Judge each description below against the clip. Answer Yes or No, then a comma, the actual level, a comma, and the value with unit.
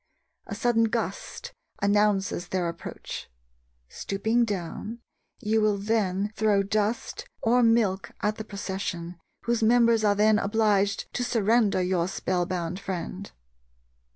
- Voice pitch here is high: Yes, high, 205 Hz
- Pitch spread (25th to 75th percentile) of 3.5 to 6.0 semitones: No, average, 2.8 semitones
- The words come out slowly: Yes, slow, 125 wpm